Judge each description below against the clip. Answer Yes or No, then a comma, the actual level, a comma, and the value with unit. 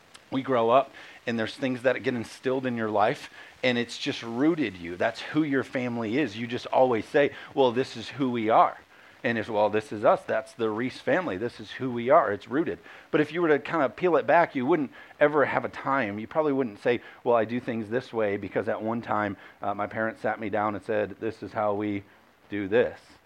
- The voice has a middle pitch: No, low, 115 Hz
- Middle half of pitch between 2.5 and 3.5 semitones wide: Yes, average, 3.1 semitones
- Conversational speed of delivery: No, fast, 240 wpm